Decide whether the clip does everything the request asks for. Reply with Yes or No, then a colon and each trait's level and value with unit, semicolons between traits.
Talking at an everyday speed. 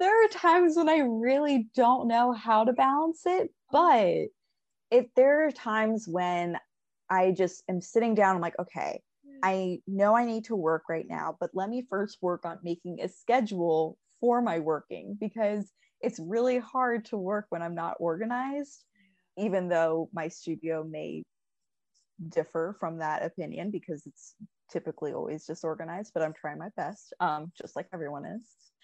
Yes: average, 165 wpm